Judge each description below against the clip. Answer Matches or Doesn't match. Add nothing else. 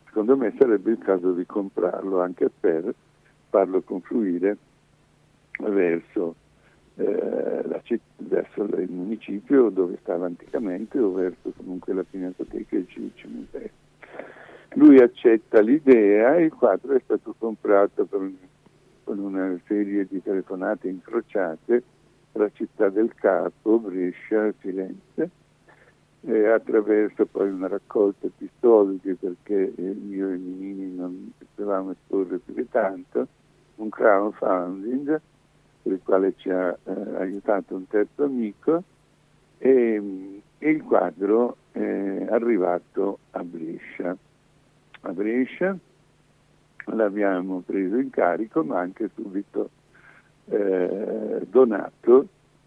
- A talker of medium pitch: Doesn't match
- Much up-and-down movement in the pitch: Matches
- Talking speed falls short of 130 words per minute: Matches